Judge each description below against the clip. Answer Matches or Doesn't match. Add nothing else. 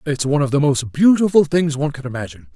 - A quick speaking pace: Matches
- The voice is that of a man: Matches